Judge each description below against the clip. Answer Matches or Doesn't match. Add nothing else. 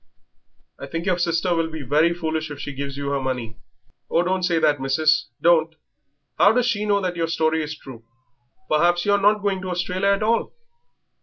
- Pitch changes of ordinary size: Matches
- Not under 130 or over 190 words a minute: Doesn't match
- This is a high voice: Doesn't match